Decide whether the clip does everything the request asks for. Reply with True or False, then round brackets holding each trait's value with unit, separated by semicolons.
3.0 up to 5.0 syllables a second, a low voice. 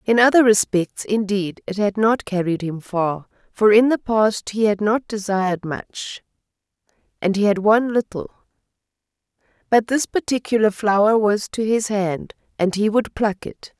False (4.5 syllables/s; 210 Hz)